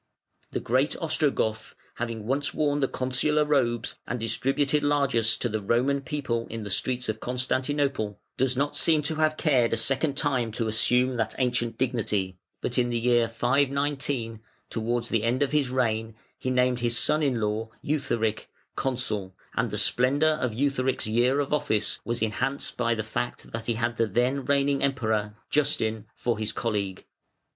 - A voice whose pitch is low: Yes, low, 125 Hz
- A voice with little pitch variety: No, average, 3.5 semitones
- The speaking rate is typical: Yes, average, 170 wpm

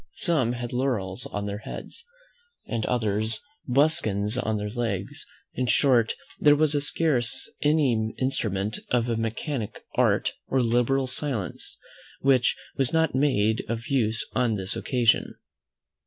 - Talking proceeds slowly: Yes, slow, 130 wpm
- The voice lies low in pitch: Yes, low, 120 Hz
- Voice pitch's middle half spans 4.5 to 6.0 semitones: No, average, 3.7 semitones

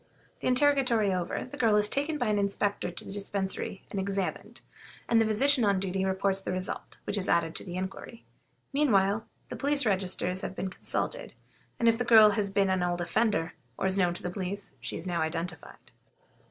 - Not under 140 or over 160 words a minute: No, average, 200 wpm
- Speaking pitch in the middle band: No, high, 200 Hz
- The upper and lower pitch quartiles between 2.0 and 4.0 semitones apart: Yes, average, 3.4 semitones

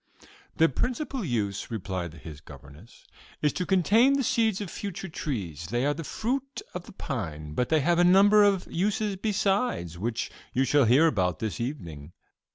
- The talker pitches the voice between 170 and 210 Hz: No, medium, 150 Hz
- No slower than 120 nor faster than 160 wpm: No, average, 170 wpm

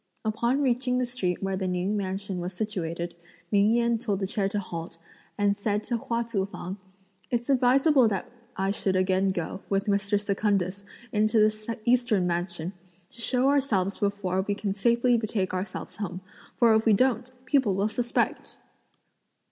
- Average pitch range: Yes, average, 3.6 semitones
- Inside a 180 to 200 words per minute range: No, average, 165 wpm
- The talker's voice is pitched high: Yes, high, 205 Hz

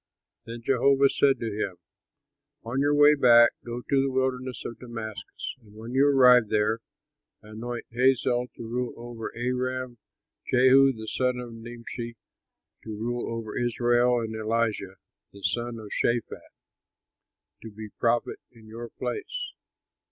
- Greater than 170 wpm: No, average, 140 wpm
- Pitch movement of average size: No, narrow, 2.2 semitones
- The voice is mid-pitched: No, low, 120 Hz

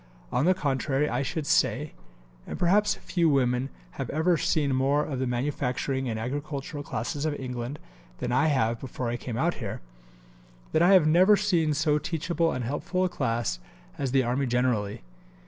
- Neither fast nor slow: Yes, average, 175 wpm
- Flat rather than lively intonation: No, average, 4.3 semitones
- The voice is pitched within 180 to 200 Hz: No, medium, 140 Hz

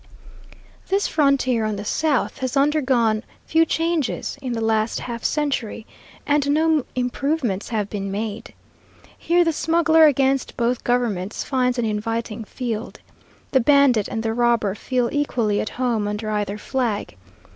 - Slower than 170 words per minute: Yes, average, 145 wpm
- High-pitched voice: Yes, high, 245 Hz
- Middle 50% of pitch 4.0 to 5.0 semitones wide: Yes, average, 4.6 semitones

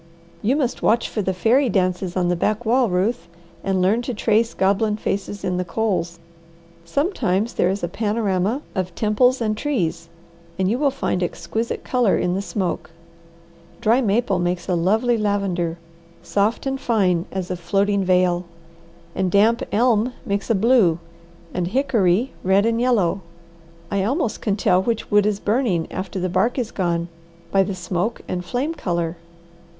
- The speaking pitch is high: Yes, high, 200 Hz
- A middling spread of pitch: Yes, average, 4.1 semitones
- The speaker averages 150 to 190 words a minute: Yes, average, 165 wpm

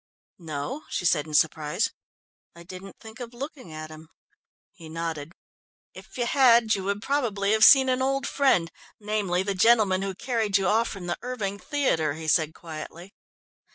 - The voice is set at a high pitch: Yes, high, 195 Hz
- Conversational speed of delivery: Yes, average, 170 wpm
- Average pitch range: No, wide, 6.2 semitones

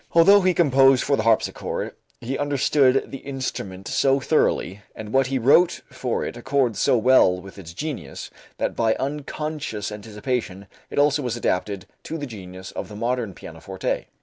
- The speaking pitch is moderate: No, low, 125 Hz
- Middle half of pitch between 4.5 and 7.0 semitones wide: Yes, average, 5.1 semitones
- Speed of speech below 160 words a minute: No, average, 165 wpm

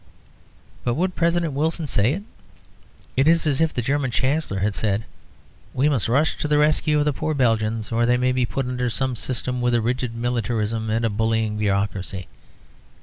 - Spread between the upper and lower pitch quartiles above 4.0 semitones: Yes, average, 4.6 semitones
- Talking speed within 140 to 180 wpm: No, average, 190 wpm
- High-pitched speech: No, low, 125 Hz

